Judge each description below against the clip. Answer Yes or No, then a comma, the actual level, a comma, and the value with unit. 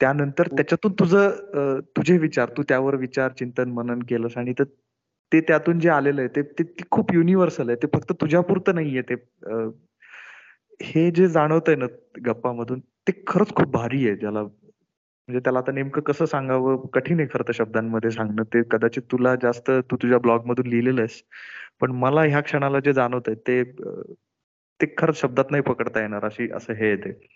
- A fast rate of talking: Yes, fast, 185 wpm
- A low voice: Yes, low, 130 Hz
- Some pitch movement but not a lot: Yes, average, 4.5 semitones